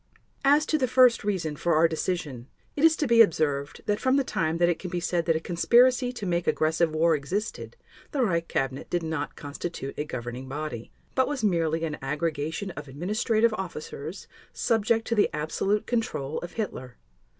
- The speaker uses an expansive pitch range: Yes, wide, 6.6 semitones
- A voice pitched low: No, medium, 170 Hz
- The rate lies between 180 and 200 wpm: Yes, average, 185 wpm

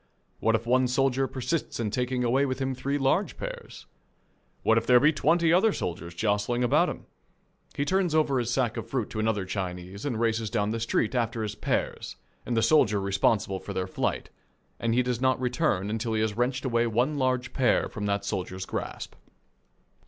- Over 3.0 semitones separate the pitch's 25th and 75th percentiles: Yes, average, 3.7 semitones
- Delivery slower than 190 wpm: No, average, 195 wpm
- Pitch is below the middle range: Yes, low, 120 Hz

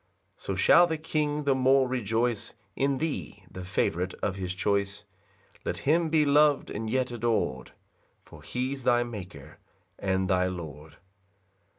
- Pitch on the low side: Yes, low, 120 Hz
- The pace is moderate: Yes, average, 150 wpm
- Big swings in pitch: Yes, wide, 6.7 semitones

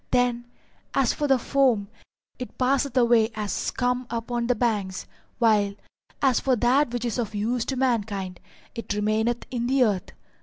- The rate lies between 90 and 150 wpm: No, average, 160 wpm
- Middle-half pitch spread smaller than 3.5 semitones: Yes, average, 2.7 semitones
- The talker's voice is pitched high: Yes, high, 240 Hz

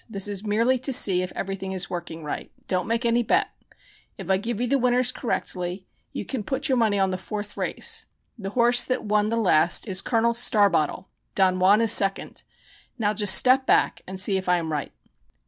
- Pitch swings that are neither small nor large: Yes, average, 3.8 semitones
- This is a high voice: Yes, high, 205 Hz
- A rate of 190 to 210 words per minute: Yes, fast, 205 wpm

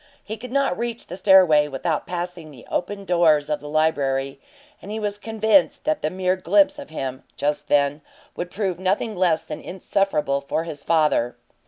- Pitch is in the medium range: Yes, medium, 175 Hz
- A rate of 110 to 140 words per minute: No, average, 180 wpm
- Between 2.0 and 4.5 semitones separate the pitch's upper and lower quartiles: No, average, 5.0 semitones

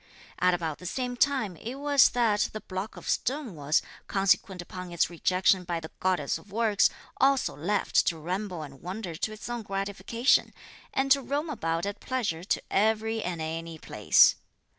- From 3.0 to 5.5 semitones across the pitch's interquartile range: Yes, average, 5.2 semitones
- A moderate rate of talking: Yes, average, 175 wpm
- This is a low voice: No, high, 195 Hz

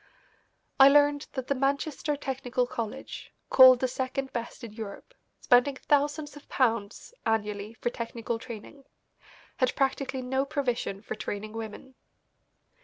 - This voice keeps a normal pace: No, slow, 130 wpm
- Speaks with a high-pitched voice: Yes, very high, 255 Hz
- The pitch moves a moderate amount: Yes, average, 3.3 semitones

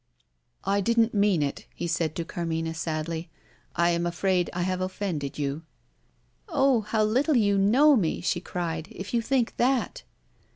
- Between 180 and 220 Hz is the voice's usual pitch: Yes, medium, 185 Hz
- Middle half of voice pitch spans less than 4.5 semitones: No, average, 5.2 semitones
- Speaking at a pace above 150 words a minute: Yes, average, 160 wpm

